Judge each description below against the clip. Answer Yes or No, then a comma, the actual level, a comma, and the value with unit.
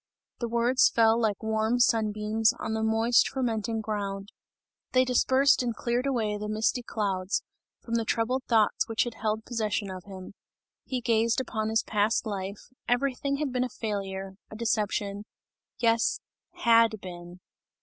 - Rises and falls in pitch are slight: Yes, narrow, 2.2 semitones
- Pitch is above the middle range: Yes, high, 220 Hz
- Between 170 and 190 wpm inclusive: No, average, 155 wpm